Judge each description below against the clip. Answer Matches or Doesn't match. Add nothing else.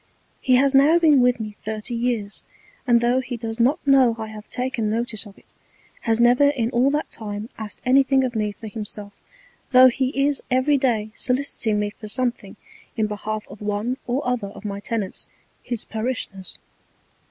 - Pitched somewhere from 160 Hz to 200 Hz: Doesn't match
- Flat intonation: Doesn't match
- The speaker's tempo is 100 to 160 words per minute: Doesn't match